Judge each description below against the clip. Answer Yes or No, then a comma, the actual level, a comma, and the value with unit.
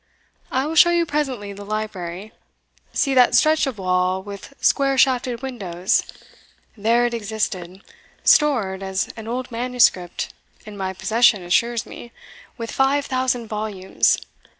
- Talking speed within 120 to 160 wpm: Yes, slow, 135 wpm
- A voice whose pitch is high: Yes, high, 230 Hz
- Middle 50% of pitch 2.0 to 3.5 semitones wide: No, average, 4.9 semitones